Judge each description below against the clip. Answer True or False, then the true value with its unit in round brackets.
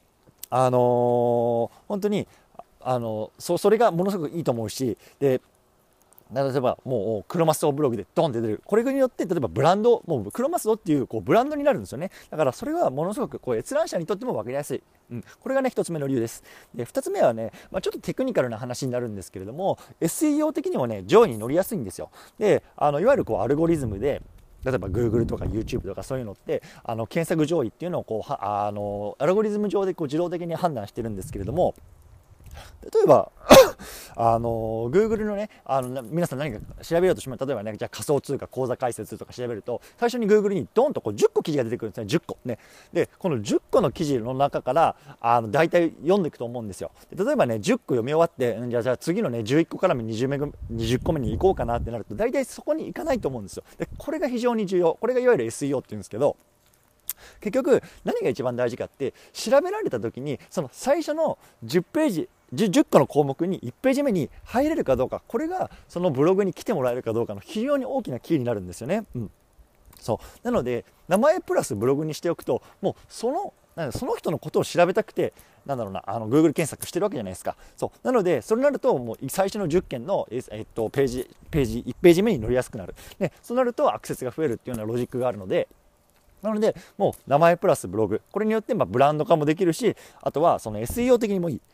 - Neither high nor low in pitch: True (145 Hz)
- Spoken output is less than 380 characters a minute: False (460 characters per minute)